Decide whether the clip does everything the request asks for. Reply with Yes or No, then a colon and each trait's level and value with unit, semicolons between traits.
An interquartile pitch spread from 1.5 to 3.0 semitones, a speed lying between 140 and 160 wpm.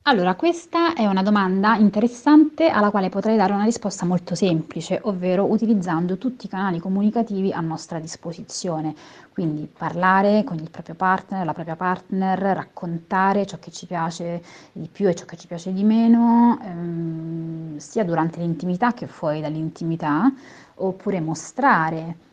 No: average, 4.0 semitones; average, 150 wpm